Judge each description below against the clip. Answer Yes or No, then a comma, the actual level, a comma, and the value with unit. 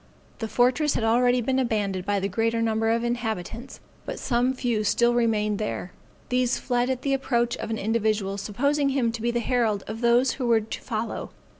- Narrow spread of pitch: Yes, narrow, 2.2 semitones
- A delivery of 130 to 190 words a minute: No, average, 200 wpm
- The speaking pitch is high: Yes, high, 235 Hz